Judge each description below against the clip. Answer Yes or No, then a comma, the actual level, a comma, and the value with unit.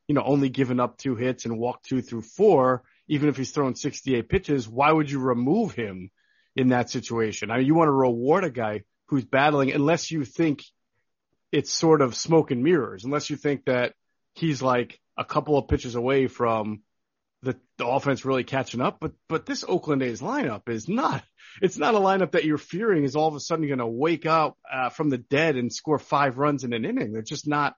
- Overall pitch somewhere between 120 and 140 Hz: Yes, low, 135 Hz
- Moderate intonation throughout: Yes, average, 3.7 semitones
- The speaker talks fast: Yes, fast, 215 wpm